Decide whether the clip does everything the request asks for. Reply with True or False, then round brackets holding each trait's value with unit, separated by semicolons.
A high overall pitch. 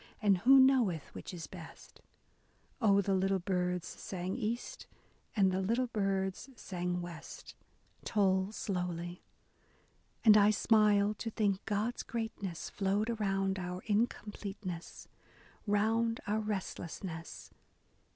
True (200 Hz)